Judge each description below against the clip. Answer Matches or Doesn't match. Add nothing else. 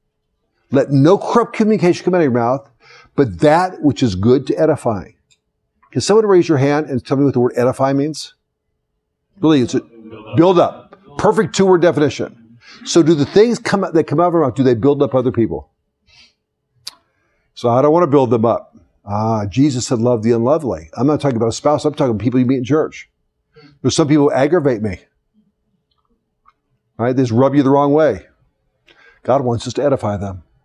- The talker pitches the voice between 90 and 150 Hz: Matches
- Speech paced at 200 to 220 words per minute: Matches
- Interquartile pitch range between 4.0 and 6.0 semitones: Matches